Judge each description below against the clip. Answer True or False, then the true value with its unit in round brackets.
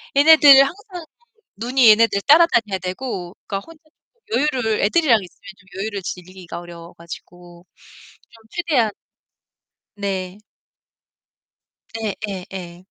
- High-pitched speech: True (215 Hz)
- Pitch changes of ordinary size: False (7.1 semitones)